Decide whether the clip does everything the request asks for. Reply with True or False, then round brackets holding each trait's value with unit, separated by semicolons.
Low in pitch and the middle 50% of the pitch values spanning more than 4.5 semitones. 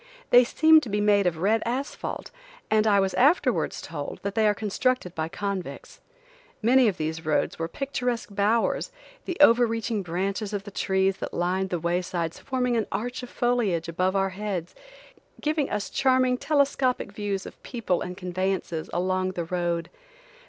False (200 Hz; 5.1 semitones)